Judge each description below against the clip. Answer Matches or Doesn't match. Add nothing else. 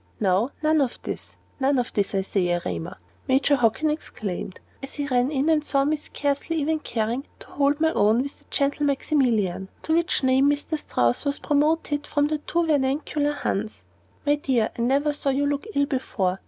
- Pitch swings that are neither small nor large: Matches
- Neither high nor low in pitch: Doesn't match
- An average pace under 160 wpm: Doesn't match